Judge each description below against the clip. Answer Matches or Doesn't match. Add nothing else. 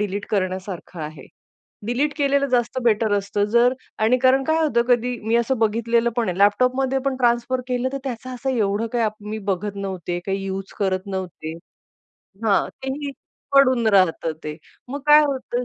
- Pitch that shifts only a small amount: Doesn't match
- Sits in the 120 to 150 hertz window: Doesn't match